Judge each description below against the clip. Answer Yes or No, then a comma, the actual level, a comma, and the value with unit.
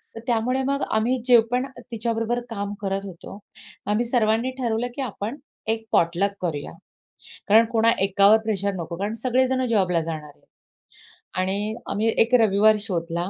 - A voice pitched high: Yes, high, 215 Hz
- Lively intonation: No, average, 3.4 semitones